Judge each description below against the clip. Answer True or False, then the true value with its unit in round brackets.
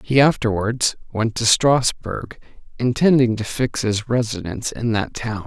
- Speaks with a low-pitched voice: True (115 Hz)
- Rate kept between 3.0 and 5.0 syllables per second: True (4.4 syllables/s)